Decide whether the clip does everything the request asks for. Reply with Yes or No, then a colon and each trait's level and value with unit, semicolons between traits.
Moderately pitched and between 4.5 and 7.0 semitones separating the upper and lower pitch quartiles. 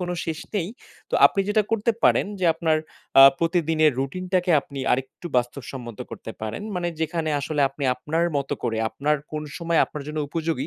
No: medium, 155 Hz; average, 4.0 semitones